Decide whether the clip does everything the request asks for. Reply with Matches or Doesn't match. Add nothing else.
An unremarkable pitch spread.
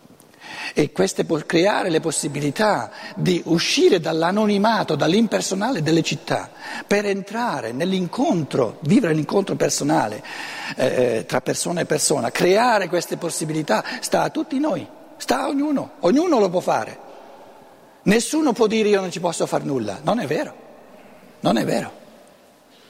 Doesn't match